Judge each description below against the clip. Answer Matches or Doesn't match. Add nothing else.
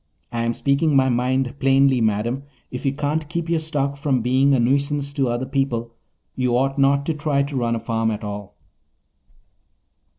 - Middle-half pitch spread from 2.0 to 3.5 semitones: Matches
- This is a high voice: Doesn't match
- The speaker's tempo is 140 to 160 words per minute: Doesn't match